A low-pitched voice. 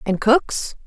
No: high, 230 Hz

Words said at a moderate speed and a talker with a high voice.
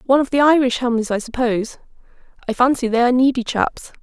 Yes: average, 195 wpm; very high, 250 Hz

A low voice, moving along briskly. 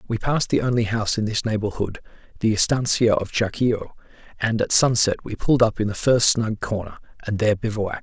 No: low, 110 Hz; average, 195 wpm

